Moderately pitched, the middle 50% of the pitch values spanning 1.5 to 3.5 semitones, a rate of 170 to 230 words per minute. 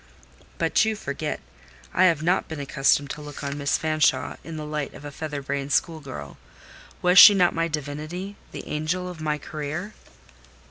Yes: medium, 155 Hz; average, 2.8 semitones; average, 175 wpm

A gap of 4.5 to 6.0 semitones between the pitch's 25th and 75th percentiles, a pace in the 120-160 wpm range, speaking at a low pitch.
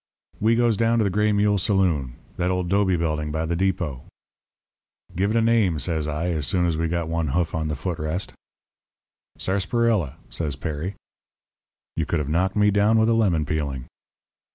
No: average, 4.8 semitones; average, 185 wpm; very low, 90 Hz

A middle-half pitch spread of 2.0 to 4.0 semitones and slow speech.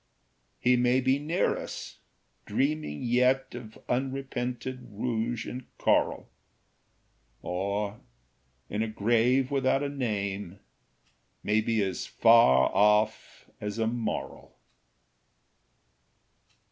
Yes: average, 3.7 semitones; slow, 95 wpm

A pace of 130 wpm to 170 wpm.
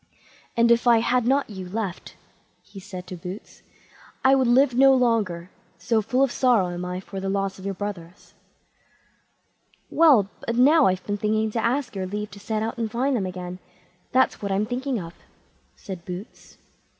No: average, 185 wpm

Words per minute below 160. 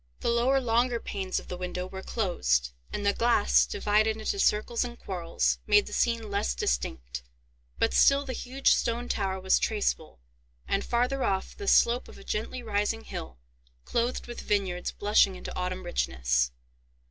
No: average, 165 wpm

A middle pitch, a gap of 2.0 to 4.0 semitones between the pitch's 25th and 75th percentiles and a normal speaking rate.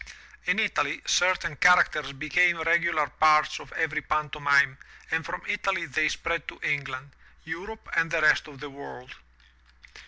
Yes: medium, 155 Hz; average, 2.8 semitones; average, 150 wpm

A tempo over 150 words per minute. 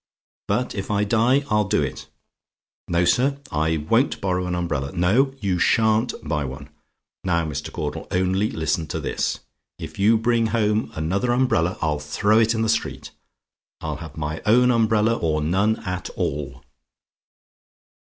Yes: average, 160 wpm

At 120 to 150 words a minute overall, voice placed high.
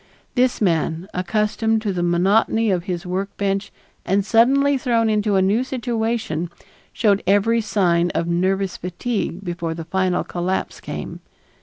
Yes: average, 140 wpm; high, 195 Hz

